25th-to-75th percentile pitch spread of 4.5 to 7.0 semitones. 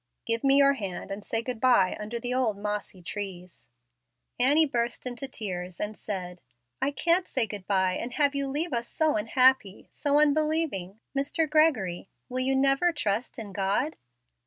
Yes: wide, 5.6 semitones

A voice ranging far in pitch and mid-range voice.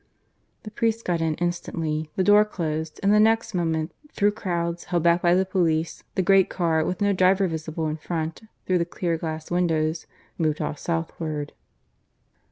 No: average, 2.8 semitones; medium, 170 Hz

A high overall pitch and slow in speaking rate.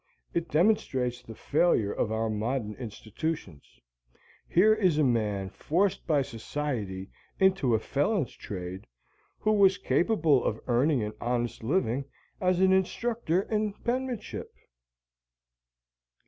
No: medium, 140 Hz; slow, 120 wpm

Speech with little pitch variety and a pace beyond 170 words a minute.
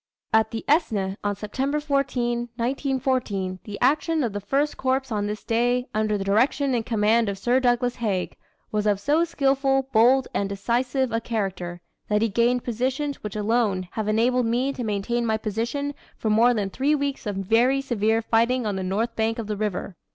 No: average, 3.8 semitones; average, 190 wpm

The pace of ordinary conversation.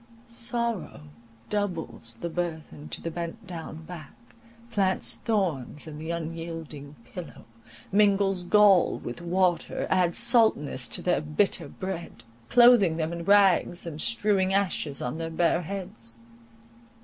No: slow, 125 wpm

